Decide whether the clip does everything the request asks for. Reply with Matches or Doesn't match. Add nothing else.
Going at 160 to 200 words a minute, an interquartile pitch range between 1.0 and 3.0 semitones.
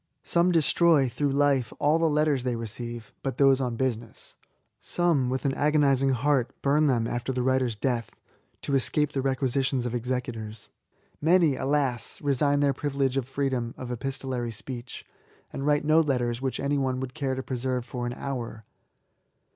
Matches